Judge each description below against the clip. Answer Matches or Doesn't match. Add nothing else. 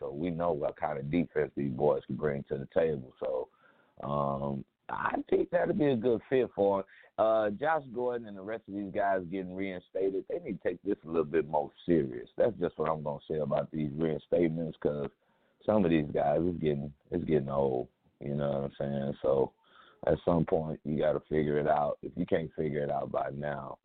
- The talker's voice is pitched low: Matches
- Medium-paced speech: Doesn't match